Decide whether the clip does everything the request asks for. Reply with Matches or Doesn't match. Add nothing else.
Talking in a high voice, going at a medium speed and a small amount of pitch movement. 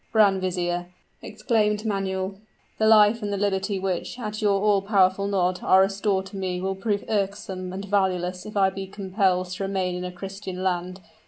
Matches